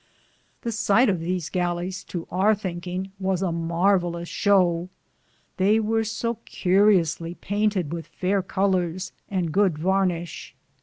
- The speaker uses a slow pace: Yes, slow, 125 wpm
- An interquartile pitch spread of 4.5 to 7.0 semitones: No, narrow, 2.6 semitones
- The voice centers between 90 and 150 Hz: No, medium, 185 Hz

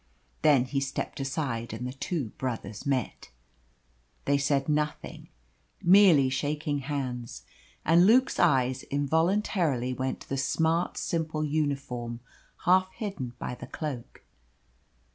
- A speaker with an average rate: No, slow, 120 wpm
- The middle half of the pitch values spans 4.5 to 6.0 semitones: No, average, 3.9 semitones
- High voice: No, medium, 140 Hz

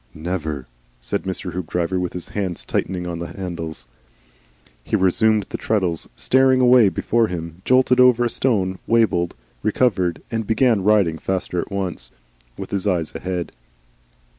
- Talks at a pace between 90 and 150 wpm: Yes, average, 145 wpm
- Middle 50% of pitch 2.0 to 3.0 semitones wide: No, average, 4.2 semitones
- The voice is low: Yes, very low, 95 Hz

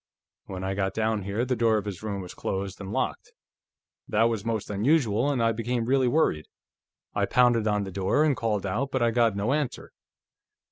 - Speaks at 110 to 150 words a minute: No, average, 200 wpm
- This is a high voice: No, low, 110 Hz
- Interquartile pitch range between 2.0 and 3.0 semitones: No, average, 3.6 semitones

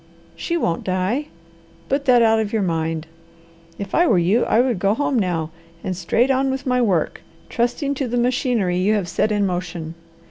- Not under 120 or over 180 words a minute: No, average, 200 wpm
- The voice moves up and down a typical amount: No, wide, 5.7 semitones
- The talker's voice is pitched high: Yes, high, 215 Hz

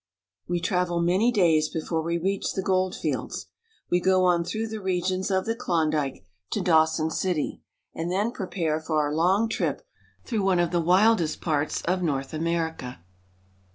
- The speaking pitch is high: No, medium, 175 Hz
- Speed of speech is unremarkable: Yes, average, 165 wpm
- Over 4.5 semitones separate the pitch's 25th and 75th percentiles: No, average, 2.8 semitones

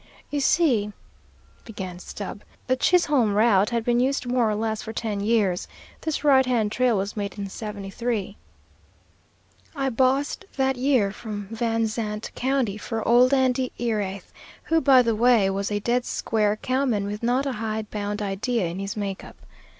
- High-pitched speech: Yes, high, 225 Hz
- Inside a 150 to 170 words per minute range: Yes, average, 165 wpm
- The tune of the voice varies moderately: Yes, average, 3.6 semitones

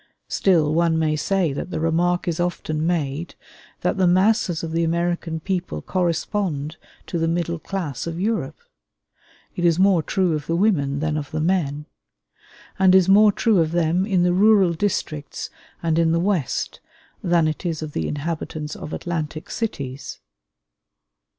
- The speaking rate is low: No, average, 160 wpm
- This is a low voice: No, medium, 170 Hz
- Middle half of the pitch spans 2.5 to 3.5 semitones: Yes, average, 2.8 semitones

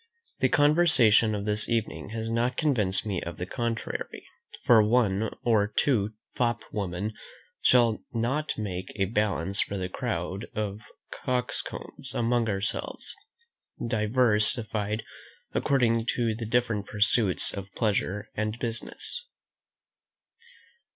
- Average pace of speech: No, slow, 115 wpm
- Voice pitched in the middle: No, low, 110 Hz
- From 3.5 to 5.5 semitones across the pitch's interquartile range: No, narrow, 2.6 semitones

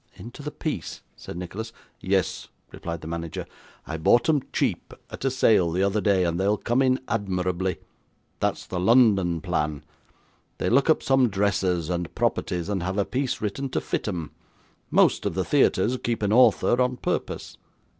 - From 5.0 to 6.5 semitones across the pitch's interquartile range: Yes, wide, 5.6 semitones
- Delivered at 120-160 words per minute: No, average, 175 wpm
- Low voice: Yes, low, 100 Hz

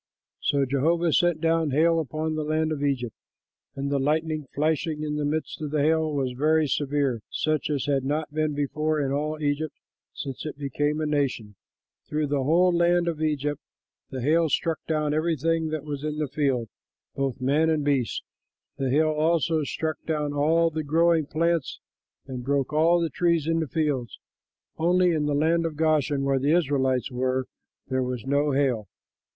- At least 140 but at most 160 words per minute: No, average, 180 wpm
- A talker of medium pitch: Yes, medium, 150 Hz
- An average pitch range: No, narrow, 2.3 semitones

